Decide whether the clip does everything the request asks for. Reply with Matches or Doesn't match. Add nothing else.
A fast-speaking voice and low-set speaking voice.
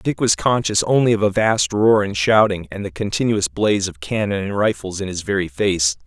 Matches